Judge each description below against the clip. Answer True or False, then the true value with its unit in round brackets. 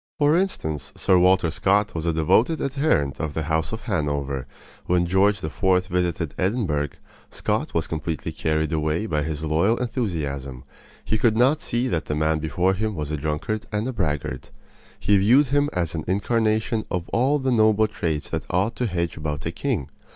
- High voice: False (90 Hz)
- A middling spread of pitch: False (6.0 semitones)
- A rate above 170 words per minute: True (180 wpm)